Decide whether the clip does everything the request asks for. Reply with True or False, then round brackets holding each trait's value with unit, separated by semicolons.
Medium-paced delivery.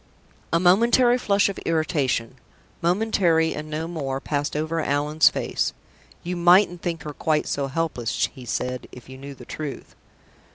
True (155 wpm)